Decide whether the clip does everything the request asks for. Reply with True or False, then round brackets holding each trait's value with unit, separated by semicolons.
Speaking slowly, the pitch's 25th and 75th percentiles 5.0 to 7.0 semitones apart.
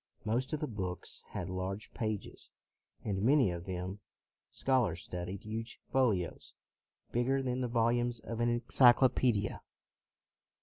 False (130 wpm; 4.4 semitones)